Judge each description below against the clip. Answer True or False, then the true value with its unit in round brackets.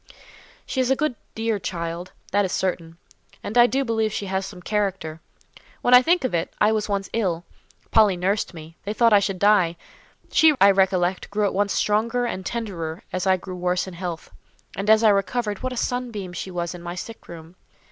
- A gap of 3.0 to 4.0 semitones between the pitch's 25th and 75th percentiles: True (3.7 semitones)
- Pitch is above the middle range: True (195 Hz)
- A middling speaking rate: False (210 wpm)